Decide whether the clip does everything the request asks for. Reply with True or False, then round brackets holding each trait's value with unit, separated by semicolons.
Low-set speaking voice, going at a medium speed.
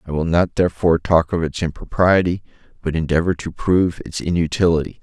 True (85 Hz; 165 wpm)